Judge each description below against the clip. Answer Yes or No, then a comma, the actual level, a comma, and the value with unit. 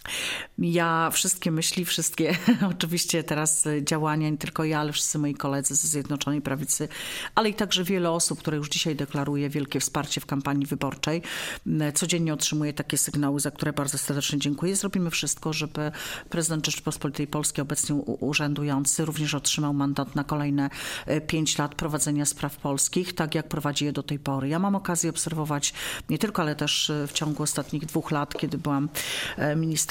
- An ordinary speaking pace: No, fast, 165 wpm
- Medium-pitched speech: Yes, medium, 150 Hz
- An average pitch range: No, narrow, 2.1 semitones